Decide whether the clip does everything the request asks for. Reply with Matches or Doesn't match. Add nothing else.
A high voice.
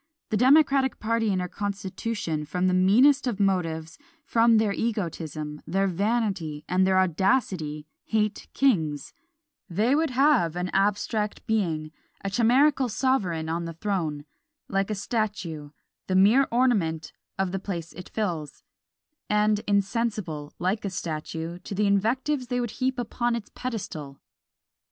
Matches